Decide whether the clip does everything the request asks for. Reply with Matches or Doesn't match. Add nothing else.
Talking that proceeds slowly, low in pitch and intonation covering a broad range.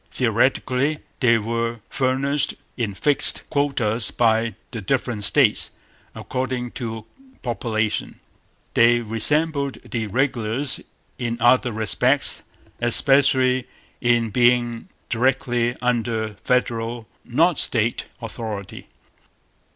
Doesn't match